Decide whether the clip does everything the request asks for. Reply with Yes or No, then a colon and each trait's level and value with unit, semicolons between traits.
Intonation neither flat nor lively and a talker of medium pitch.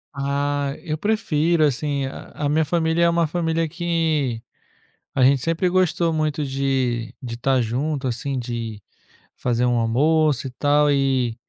Yes: average, 3.8 semitones; medium, 145 Hz